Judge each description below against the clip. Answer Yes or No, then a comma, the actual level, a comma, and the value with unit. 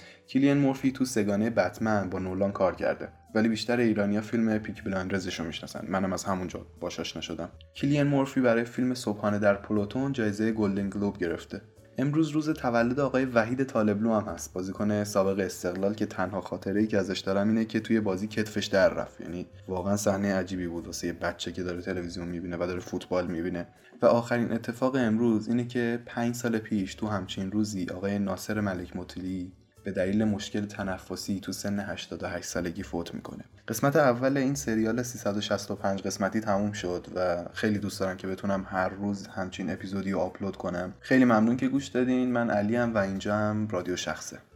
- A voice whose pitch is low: Yes, low, 100 Hz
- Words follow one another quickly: Yes, fast, 180 wpm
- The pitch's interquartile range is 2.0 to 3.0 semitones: No, average, 3.6 semitones